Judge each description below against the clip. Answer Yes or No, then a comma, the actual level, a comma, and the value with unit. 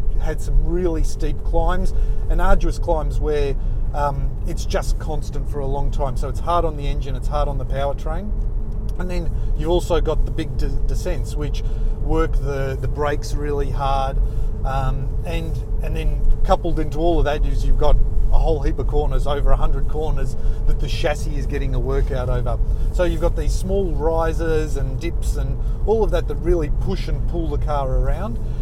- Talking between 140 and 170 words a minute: No, average, 195 wpm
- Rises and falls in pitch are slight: No, average, 4.5 semitones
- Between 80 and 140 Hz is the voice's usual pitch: Yes, low, 135 Hz